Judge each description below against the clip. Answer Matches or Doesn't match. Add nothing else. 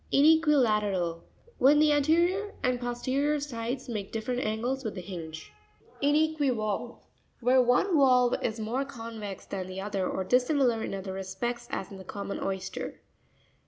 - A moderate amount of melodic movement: Doesn't match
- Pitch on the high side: Matches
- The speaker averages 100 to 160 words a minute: Matches